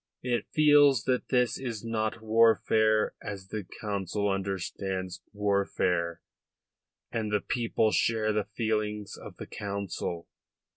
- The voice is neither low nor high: No, low, 105 Hz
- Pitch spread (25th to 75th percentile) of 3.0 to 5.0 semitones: No, narrow, 2.4 semitones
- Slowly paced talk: Yes, slow, 115 wpm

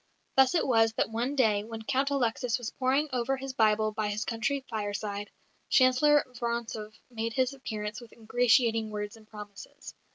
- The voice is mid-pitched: No, high, 225 Hz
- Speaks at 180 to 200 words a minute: No, average, 165 wpm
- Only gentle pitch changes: No, average, 3.1 semitones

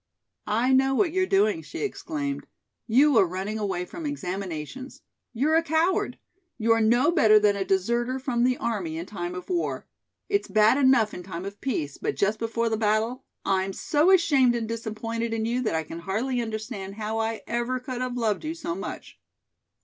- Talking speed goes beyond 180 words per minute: Yes, average, 190 wpm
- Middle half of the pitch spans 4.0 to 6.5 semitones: Yes, average, 4.6 semitones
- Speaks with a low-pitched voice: No, high, 230 Hz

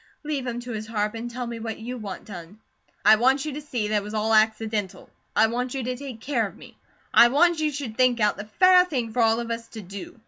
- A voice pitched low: No, high, 230 Hz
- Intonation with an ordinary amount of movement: Yes, average, 3.0 semitones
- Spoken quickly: Yes, fast, 265 wpm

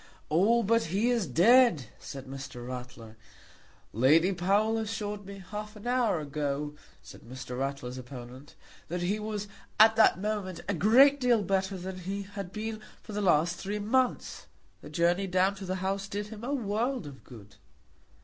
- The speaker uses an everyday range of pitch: No, wide, 6.1 semitones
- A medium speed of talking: Yes, average, 170 wpm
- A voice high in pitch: Yes, high, 195 Hz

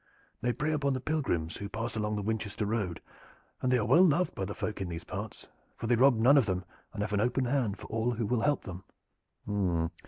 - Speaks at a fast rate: Yes, fast, 230 wpm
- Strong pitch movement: No, average, 4.1 semitones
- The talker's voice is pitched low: Yes, low, 110 Hz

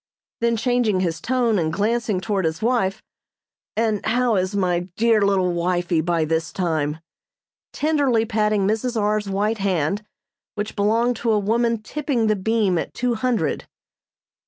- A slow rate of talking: No, average, 150 wpm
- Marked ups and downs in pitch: No, average, 4.0 semitones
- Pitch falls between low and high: No, high, 210 Hz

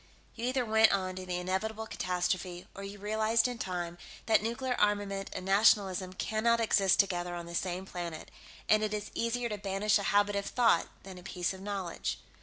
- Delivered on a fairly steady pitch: No, average, 3.0 semitones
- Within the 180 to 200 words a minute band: Yes, average, 195 wpm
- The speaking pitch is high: Yes, high, 200 Hz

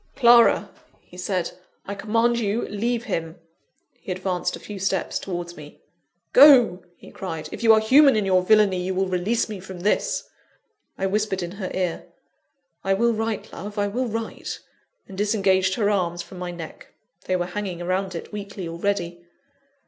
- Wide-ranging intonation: No, average, 3.1 semitones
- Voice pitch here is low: No, high, 195 Hz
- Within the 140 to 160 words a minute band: No, average, 170 wpm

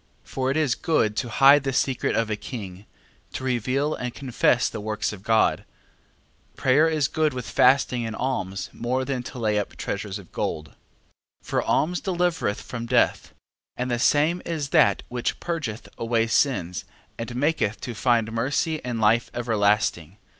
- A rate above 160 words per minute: Yes, average, 175 wpm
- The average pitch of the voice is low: Yes, low, 120 Hz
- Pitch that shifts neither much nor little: Yes, average, 4.2 semitones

